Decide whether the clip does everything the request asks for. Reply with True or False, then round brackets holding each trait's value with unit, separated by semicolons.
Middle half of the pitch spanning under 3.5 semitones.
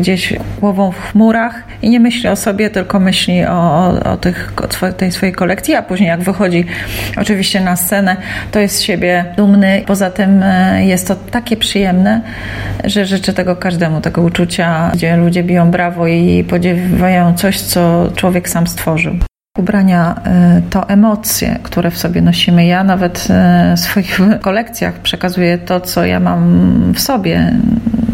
True (2.6 semitones)